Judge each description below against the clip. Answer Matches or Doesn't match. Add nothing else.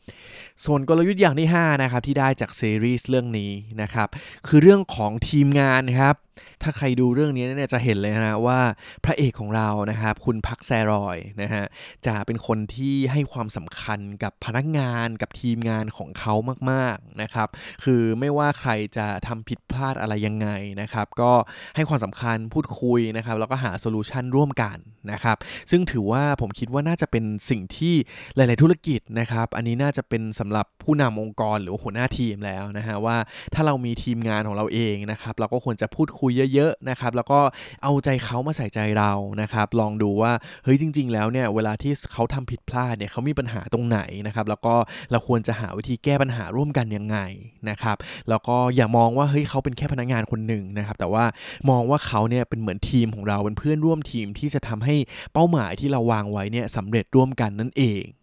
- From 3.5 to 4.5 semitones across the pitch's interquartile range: Matches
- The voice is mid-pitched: Doesn't match